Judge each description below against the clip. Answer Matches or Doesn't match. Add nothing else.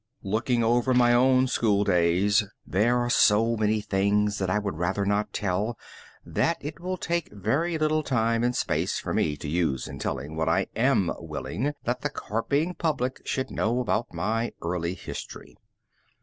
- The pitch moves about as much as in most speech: Matches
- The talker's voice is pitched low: Matches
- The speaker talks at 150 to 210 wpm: Matches